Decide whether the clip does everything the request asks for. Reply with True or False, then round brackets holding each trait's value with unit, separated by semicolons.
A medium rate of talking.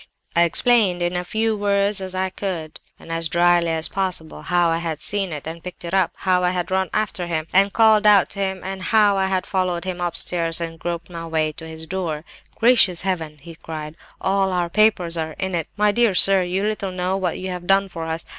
False (230 wpm)